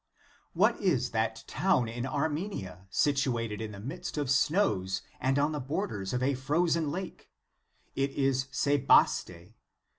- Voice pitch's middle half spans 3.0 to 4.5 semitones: No, average, 5.0 semitones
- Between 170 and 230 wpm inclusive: No, average, 145 wpm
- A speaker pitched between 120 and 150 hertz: Yes, low, 135 Hz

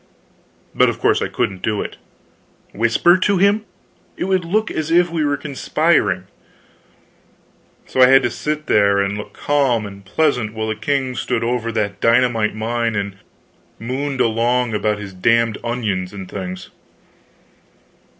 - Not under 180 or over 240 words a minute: No, average, 150 wpm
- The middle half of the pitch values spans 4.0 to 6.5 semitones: Yes, average, 5.3 semitones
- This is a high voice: No, low, 115 Hz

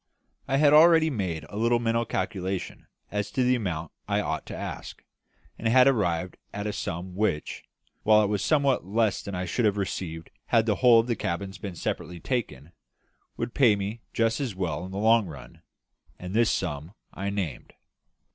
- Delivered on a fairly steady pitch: No, average, 4.3 semitones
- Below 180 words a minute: No, average, 185 wpm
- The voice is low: Yes, low, 105 Hz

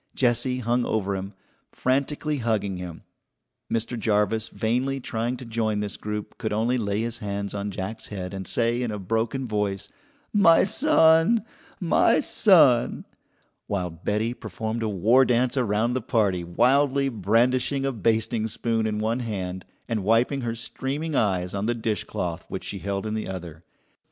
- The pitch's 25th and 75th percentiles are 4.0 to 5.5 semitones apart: No, average, 3.6 semitones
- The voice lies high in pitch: No, low, 115 Hz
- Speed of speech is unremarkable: Yes, average, 160 wpm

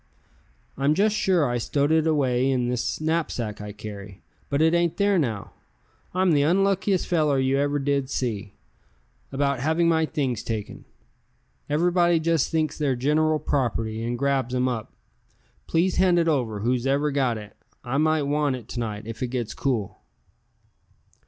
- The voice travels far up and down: No, average, 4.7 semitones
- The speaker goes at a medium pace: Yes, average, 160 wpm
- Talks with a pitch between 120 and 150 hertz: Yes, medium, 140 Hz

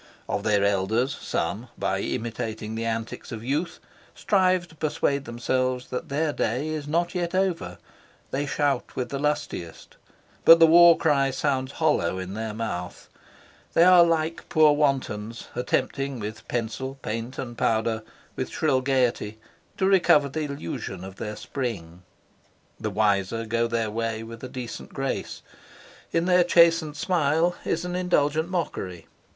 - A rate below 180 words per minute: Yes, average, 150 wpm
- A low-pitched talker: Yes, low, 130 Hz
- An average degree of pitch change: No, wide, 5.9 semitones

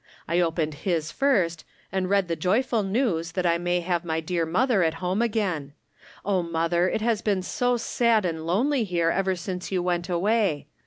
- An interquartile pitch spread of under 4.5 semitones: Yes, average, 3.8 semitones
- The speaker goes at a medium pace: Yes, average, 190 wpm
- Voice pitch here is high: No, medium, 180 Hz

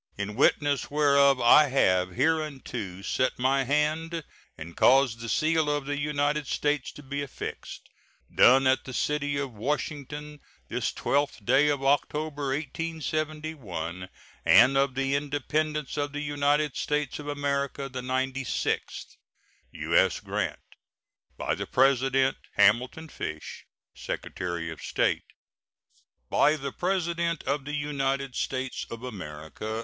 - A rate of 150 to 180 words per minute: No, slow, 135 wpm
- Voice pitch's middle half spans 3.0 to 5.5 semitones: No, narrow, 2.6 semitones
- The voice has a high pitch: No, medium, 140 Hz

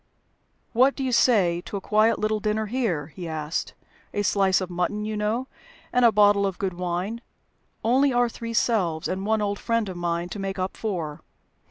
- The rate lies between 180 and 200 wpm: Yes, average, 195 wpm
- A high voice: Yes, high, 205 Hz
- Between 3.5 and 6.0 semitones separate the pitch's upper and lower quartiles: Yes, average, 4.0 semitones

